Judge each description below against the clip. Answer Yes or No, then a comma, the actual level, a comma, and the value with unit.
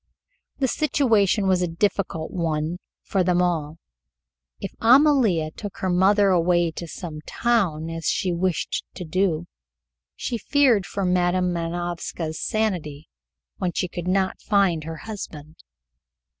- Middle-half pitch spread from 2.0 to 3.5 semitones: Yes, average, 3.2 semitones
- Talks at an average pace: No, slow, 130 wpm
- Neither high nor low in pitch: Yes, medium, 180 Hz